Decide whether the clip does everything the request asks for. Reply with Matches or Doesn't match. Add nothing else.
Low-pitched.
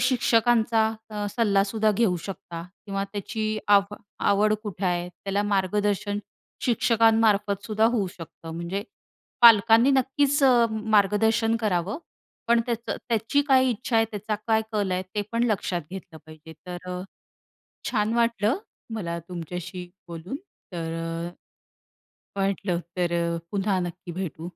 Doesn't match